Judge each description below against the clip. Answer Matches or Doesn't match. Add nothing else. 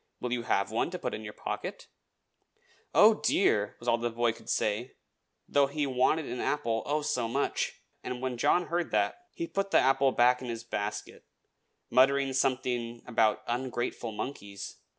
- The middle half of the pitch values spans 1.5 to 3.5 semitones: Matches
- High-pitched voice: Doesn't match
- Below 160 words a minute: Doesn't match